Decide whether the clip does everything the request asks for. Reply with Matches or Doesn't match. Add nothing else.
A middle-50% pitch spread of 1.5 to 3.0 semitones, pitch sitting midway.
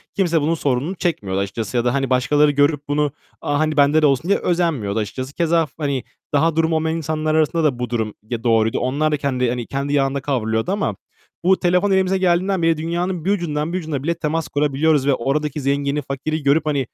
Doesn't match